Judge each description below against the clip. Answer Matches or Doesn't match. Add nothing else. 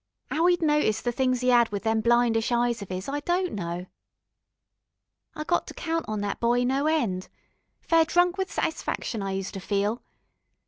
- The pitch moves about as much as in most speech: Doesn't match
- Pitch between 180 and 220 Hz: Doesn't match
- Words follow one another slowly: Doesn't match